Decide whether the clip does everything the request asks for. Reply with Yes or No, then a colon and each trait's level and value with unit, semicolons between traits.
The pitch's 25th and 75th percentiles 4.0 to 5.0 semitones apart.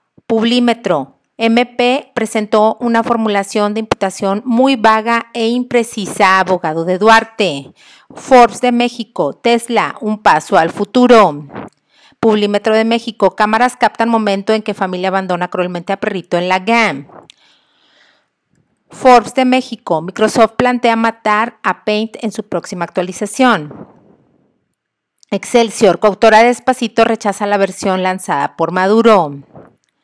No: average, 3.3 semitones